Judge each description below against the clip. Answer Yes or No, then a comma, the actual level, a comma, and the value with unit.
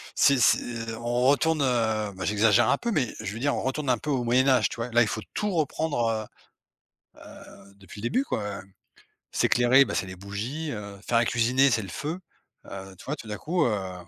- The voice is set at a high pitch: No, low, 120 Hz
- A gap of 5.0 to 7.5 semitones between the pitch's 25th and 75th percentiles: No, average, 4.5 semitones